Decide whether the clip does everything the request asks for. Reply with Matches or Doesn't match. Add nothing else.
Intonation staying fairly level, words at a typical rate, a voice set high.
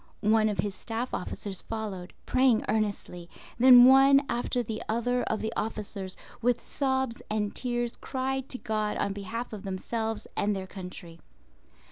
Doesn't match